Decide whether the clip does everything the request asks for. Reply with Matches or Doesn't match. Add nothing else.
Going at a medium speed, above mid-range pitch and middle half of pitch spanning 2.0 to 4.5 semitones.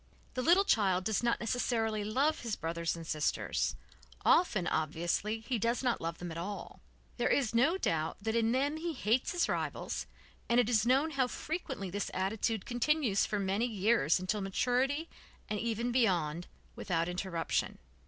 Doesn't match